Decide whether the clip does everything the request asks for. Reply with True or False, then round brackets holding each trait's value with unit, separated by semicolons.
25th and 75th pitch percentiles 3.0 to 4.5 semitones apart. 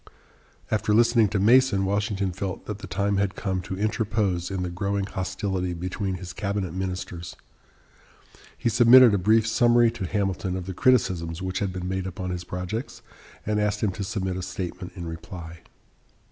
False (2.6 semitones)